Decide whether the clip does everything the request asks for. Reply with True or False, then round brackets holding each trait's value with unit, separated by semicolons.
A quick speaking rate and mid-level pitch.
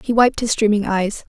False (225 wpm; 215 Hz)